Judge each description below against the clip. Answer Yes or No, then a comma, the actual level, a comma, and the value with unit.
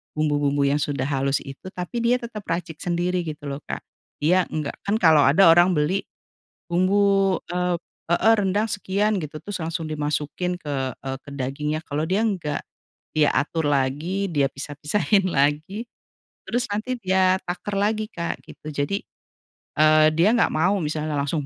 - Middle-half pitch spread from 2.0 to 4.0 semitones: No, average, 4.7 semitones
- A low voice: No, medium, 165 Hz